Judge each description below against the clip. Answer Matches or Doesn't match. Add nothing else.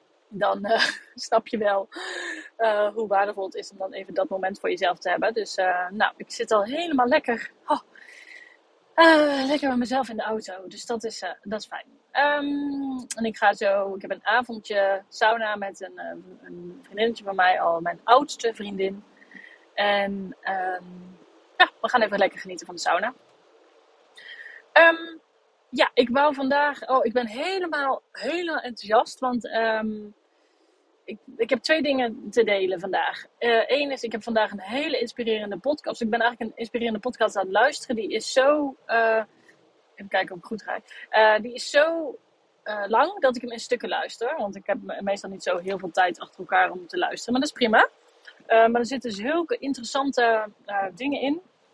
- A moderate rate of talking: Matches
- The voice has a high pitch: Matches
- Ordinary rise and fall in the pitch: Doesn't match